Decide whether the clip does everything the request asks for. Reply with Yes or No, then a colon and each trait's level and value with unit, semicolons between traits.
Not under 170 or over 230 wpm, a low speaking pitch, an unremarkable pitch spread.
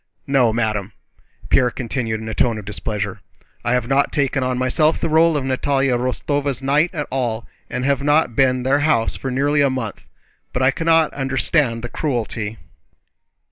Yes: average, 180 wpm; low, 130 Hz; average, 3.5 semitones